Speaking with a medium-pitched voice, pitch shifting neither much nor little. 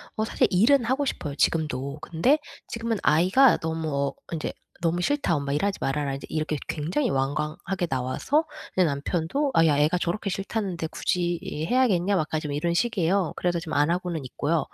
Yes: medium, 170 Hz; average, 4.8 semitones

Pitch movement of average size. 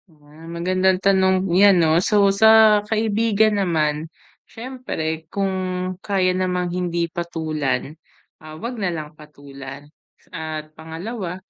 Yes: average, 4.0 semitones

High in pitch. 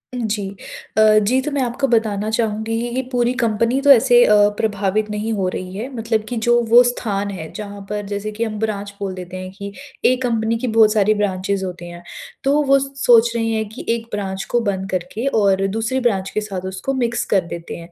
Yes: high, 215 Hz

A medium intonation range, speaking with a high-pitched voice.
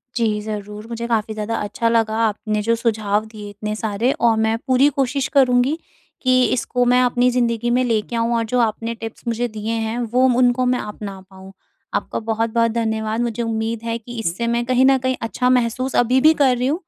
No: narrow, 2.3 semitones; high, 230 Hz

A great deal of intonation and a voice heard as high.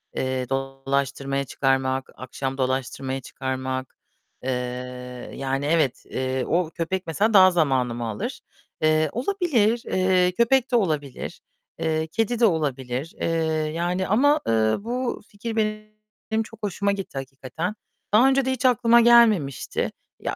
No: wide, 8.4 semitones; medium, 165 Hz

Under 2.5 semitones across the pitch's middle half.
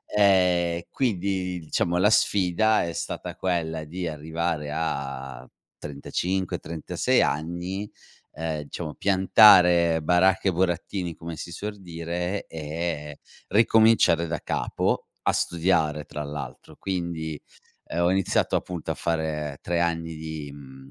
No: average, 2.8 semitones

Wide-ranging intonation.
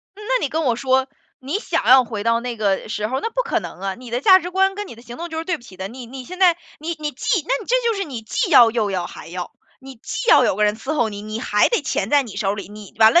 Yes: wide, 7.8 semitones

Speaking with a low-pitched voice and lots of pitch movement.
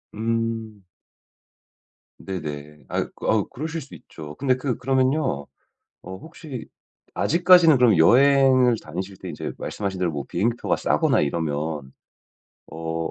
Yes: low, 110 Hz; wide, 8.4 semitones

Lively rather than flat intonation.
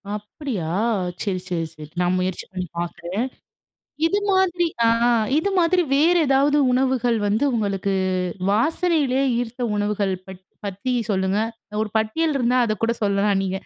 Yes: wide, 6.1 semitones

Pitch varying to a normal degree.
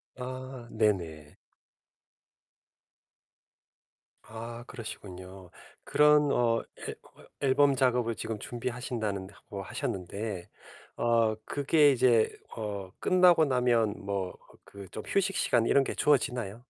Yes: average, 4.4 semitones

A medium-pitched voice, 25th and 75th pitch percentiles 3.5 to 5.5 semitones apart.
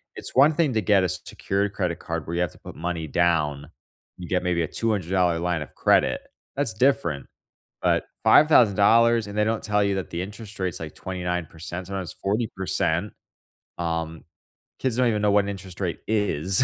No: very low, 95 Hz; average, 3.8 semitones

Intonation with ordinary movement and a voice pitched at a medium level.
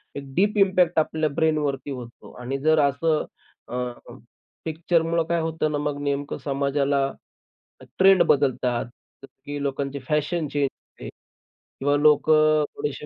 No: narrow, 2.3 semitones; medium, 150 Hz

